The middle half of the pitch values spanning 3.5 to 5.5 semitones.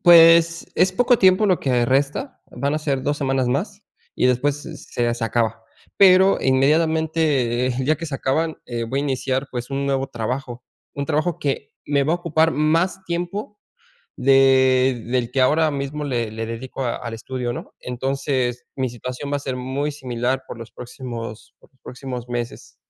Yes: average, 3.9 semitones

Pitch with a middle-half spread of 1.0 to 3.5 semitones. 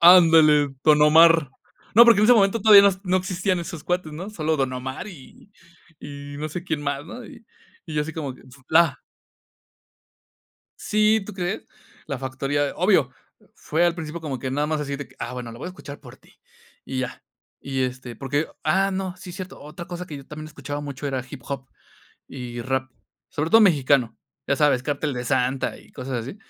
No: average, 4.8 semitones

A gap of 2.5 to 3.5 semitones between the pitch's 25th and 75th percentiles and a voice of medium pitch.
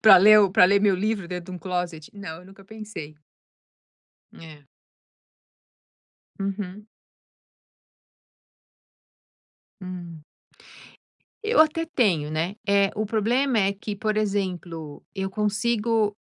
No: average, 3.1 semitones; high, 200 Hz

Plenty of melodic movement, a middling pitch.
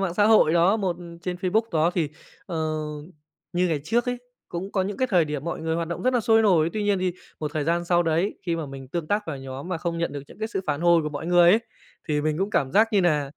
No: average, 3.9 semitones; medium, 175 Hz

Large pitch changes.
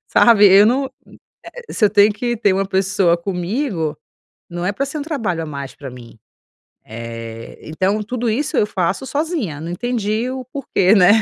Yes: wide, 6.2 semitones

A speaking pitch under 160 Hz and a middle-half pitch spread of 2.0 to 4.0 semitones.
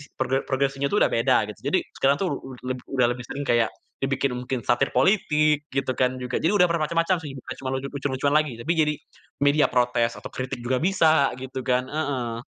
Yes: low, 135 Hz; average, 3.1 semitones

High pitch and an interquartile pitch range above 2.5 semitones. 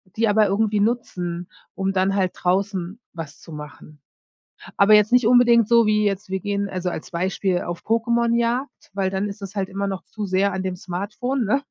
Yes: high, 200 Hz; average, 2.9 semitones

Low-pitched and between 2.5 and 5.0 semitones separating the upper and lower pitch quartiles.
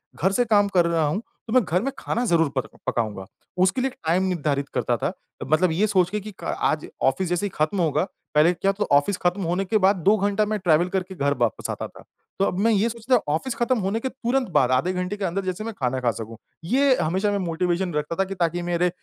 No: medium, 185 Hz; average, 4.3 semitones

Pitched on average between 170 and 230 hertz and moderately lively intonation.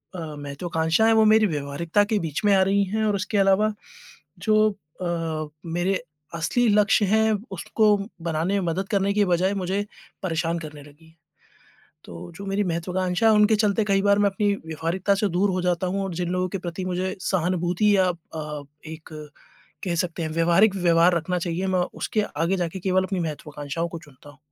Yes: medium, 185 Hz; average, 3.3 semitones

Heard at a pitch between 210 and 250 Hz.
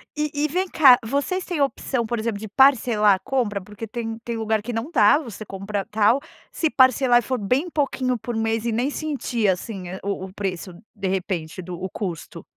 Yes: high, 225 Hz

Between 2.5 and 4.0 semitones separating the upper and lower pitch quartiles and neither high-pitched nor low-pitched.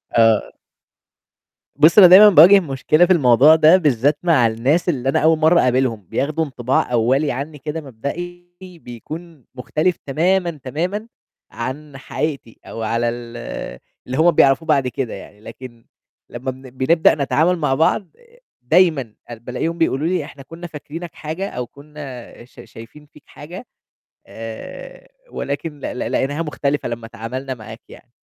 No: average, 4.7 semitones; medium, 145 Hz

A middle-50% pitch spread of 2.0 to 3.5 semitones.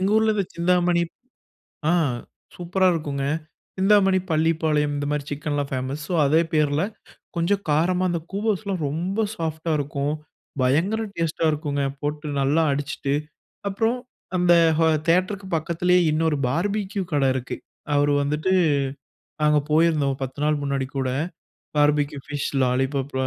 No: average, 3.9 semitones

